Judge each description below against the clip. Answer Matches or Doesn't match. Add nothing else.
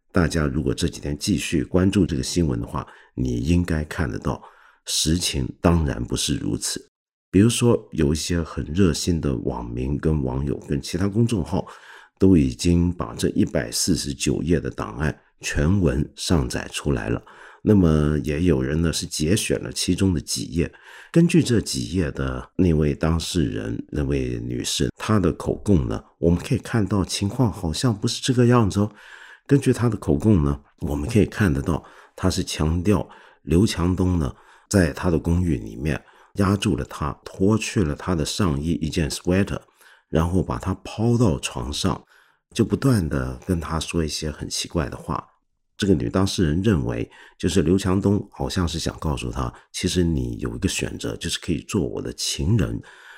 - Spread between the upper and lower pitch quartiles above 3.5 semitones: Matches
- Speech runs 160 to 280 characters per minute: Matches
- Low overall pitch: Matches